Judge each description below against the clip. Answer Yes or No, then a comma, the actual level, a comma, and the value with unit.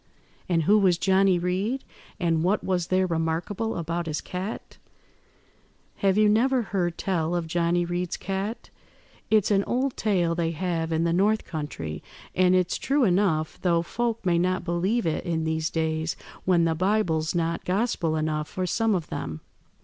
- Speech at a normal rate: Yes, average, 165 wpm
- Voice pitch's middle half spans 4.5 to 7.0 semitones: No, average, 3.2 semitones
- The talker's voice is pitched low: No, medium, 175 Hz